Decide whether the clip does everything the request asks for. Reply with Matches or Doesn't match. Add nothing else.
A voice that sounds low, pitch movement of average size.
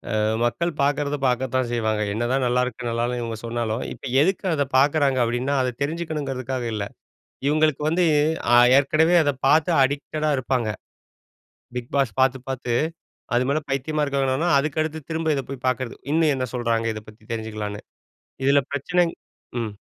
Matches